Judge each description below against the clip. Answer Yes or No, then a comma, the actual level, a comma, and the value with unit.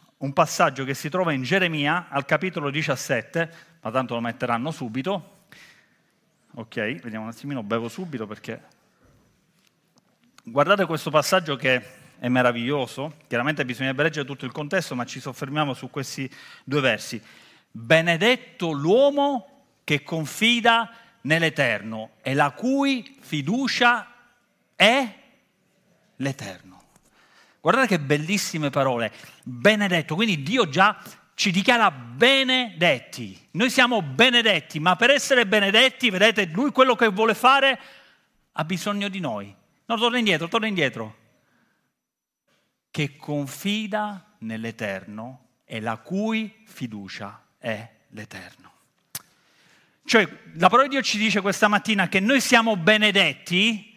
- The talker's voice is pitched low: No, medium, 175 Hz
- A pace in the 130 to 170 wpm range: No, average, 120 wpm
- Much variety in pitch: Yes, wide, 8.5 semitones